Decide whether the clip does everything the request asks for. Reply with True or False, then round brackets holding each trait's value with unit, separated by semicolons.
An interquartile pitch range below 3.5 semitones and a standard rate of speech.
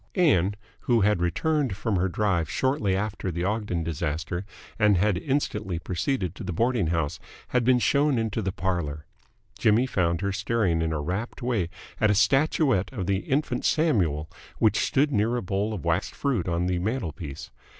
False (5.4 semitones; 175 wpm)